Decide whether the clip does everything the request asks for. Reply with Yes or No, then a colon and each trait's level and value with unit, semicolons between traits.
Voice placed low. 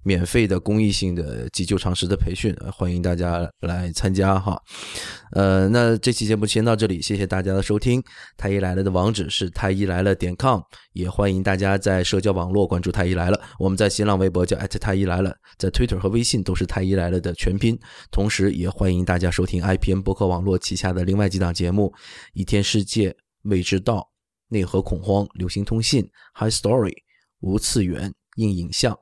Yes: very low, 95 Hz